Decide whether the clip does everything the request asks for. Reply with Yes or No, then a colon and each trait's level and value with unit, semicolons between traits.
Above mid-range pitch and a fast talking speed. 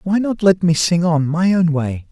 No: medium, 170 Hz; fast, 255 wpm